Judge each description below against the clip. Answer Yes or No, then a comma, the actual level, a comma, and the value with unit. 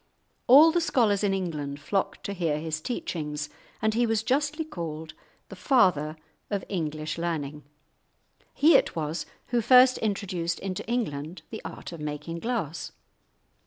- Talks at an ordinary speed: Yes, average, 145 wpm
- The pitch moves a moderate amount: No, wide, 7.1 semitones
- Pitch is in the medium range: Yes, medium, 180 Hz